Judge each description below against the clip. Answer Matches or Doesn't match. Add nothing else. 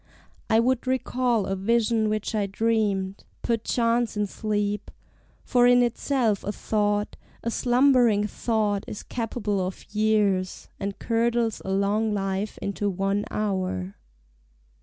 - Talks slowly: Matches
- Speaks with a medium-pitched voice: Doesn't match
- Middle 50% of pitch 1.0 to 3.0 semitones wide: Matches